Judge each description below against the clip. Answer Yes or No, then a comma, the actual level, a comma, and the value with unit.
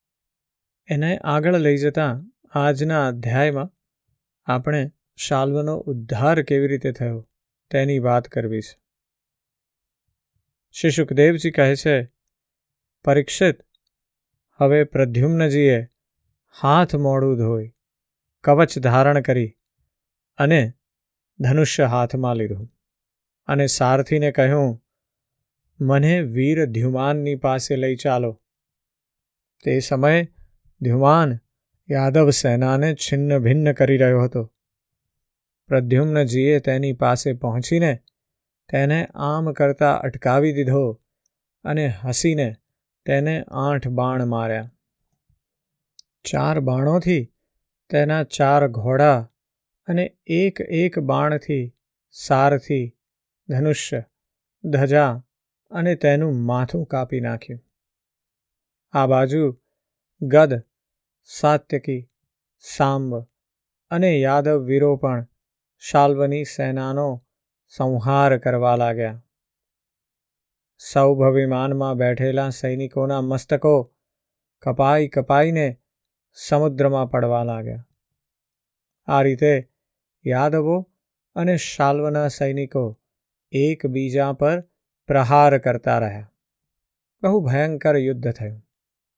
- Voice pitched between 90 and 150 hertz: Yes, medium, 140 Hz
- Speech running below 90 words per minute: Yes, average, 80 wpm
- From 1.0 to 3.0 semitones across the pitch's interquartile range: Yes, narrow, 2.6 semitones